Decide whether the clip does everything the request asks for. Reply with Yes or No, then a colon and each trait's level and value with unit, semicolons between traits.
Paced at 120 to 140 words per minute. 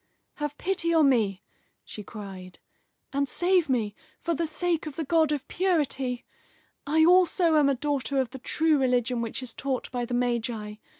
No: average, 175 wpm